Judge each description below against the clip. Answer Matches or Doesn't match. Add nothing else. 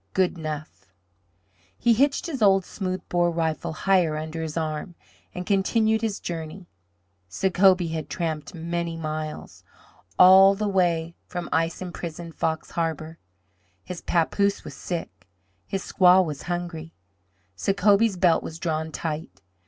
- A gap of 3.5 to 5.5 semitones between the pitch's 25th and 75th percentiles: Doesn't match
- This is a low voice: Doesn't match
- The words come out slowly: Matches